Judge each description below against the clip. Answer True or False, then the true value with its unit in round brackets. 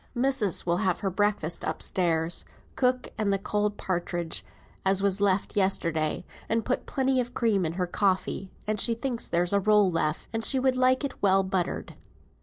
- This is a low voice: False (200 Hz)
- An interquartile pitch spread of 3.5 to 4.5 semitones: True (4.2 semitones)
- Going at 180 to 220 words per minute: True (185 wpm)